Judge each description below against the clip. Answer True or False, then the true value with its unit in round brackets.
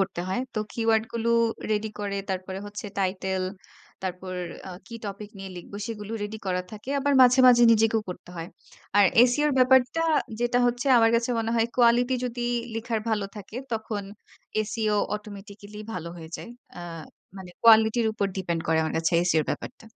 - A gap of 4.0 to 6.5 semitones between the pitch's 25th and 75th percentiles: False (3.4 semitones)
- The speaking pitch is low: False (215 Hz)